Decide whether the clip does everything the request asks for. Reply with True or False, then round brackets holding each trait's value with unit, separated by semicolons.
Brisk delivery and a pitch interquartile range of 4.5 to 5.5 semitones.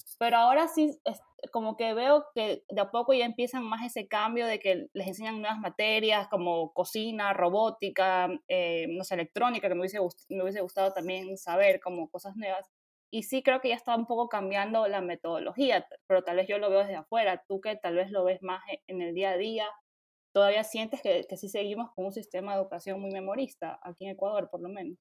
False (215 wpm; 3.2 semitones)